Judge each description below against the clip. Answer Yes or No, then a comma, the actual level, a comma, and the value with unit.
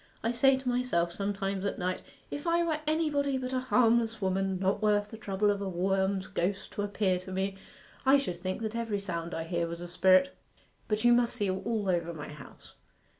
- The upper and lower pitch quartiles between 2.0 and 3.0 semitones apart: No, average, 4.3 semitones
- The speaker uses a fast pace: Yes, fast, 210 wpm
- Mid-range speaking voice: No, high, 200 Hz